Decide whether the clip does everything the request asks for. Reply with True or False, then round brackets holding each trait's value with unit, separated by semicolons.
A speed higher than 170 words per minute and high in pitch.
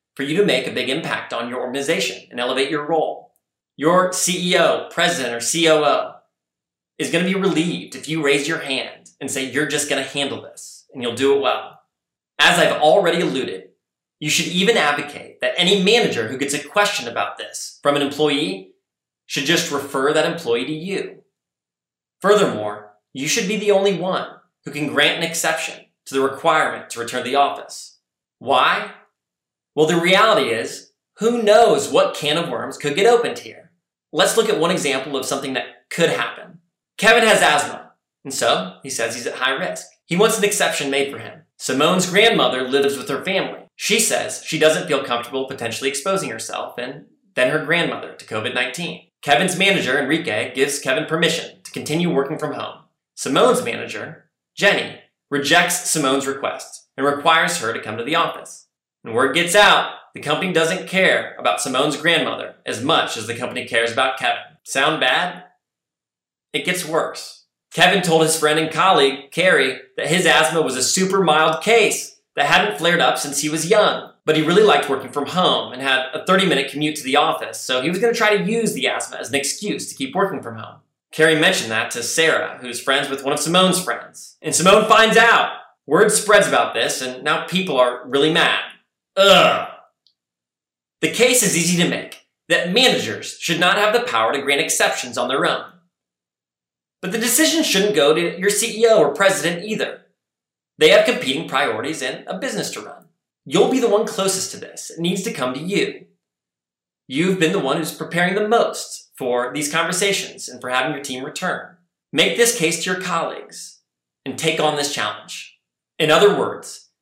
False (190 wpm; 160 Hz)